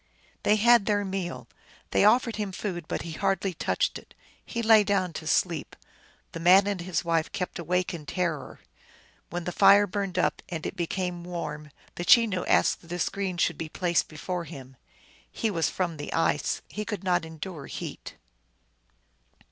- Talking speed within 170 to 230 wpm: Yes, average, 175 wpm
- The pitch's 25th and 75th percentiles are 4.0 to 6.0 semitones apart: No, average, 3.0 semitones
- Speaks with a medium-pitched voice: Yes, medium, 180 Hz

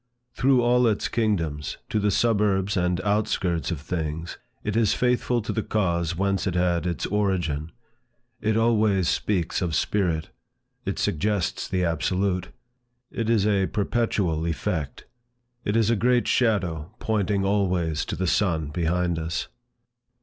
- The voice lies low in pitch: Yes, very low, 95 Hz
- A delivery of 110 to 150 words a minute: Yes, average, 140 wpm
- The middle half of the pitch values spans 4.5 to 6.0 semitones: No, average, 4.0 semitones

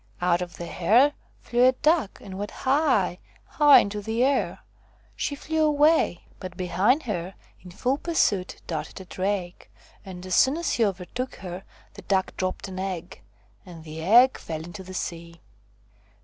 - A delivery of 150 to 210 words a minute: Yes, average, 165 wpm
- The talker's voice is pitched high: Yes, high, 195 Hz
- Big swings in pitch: Yes, wide, 6.4 semitones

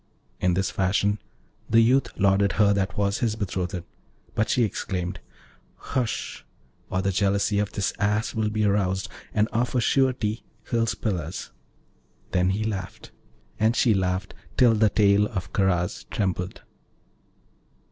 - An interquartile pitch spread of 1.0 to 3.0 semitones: Yes, narrow, 2.5 semitones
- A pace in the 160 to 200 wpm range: No, average, 145 wpm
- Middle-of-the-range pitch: No, low, 100 Hz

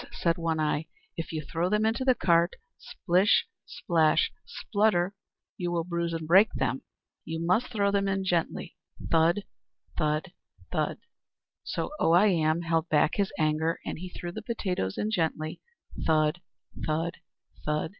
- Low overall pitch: No, medium, 170 Hz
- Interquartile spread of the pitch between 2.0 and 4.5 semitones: Yes, average, 3.3 semitones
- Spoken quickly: No, average, 155 wpm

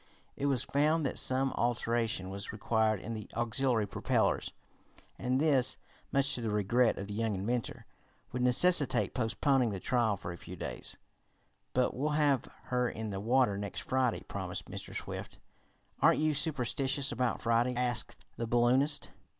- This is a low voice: Yes, low, 120 Hz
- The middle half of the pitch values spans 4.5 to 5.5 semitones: No, average, 3.3 semitones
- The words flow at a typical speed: Yes, average, 155 wpm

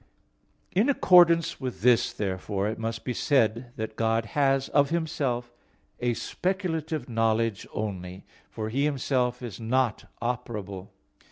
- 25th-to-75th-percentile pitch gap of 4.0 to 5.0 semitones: Yes, average, 4.5 semitones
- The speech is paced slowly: Yes, slow, 125 wpm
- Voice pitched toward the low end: Yes, low, 120 Hz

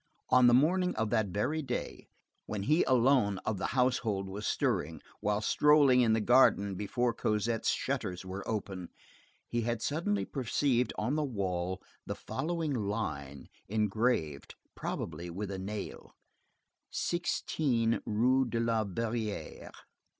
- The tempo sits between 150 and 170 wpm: No, slow, 135 wpm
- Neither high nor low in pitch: No, low, 115 Hz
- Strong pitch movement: No, average, 4.3 semitones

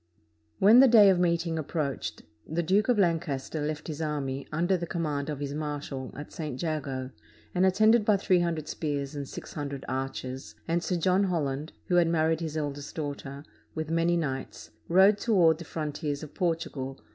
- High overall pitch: No, medium, 160 Hz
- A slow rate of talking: No, average, 180 wpm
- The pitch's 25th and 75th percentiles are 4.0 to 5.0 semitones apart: No, average, 3.5 semitones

